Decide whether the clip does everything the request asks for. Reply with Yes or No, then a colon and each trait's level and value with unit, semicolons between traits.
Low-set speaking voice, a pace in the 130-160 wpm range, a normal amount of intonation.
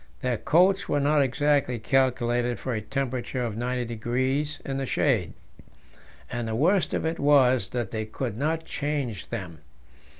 Yes: low, 130 Hz; average, 155 wpm; average, 3.5 semitones